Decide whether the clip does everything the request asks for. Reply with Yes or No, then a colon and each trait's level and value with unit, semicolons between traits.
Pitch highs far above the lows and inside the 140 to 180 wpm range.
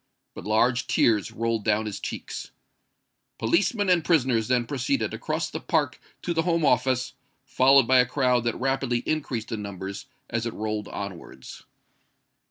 No: average, 3.7 semitones; average, 155 wpm